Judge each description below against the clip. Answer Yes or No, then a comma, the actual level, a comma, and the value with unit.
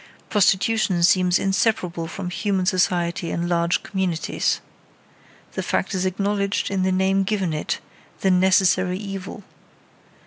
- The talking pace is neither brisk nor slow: No, slow, 125 wpm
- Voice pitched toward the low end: No, medium, 185 Hz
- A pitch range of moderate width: No, narrow, 1.7 semitones